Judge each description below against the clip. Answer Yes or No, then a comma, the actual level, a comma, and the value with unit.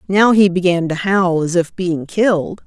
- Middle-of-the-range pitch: Yes, medium, 180 Hz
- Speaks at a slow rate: No, average, 200 wpm